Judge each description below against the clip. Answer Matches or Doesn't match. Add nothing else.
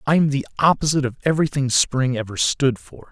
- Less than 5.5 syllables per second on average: Doesn't match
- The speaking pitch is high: Doesn't match